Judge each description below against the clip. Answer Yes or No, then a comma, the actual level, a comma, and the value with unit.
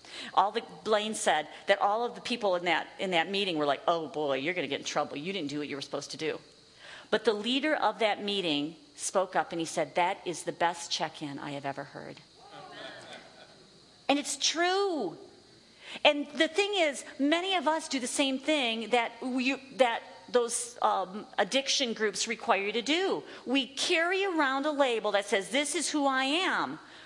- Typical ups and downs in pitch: No, wide, 8.6 semitones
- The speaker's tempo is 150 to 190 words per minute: No, average, 200 wpm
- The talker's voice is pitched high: Yes, high, 235 Hz